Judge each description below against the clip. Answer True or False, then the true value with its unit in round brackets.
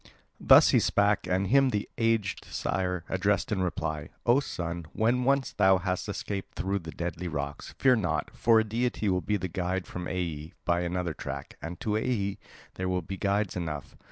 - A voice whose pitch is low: True (95 Hz)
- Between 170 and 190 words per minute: True (185 wpm)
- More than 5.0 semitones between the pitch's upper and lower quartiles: False (3.3 semitones)